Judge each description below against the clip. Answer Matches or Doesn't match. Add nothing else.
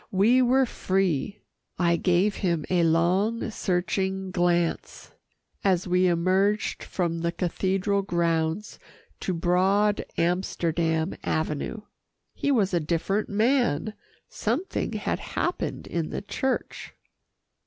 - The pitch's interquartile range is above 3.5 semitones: Doesn't match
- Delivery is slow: Matches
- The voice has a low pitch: Doesn't match